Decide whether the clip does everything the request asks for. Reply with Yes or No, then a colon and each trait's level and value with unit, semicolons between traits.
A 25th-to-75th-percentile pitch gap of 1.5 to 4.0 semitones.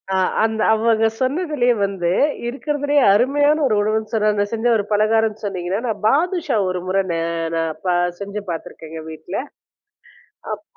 No: average, 4.5 semitones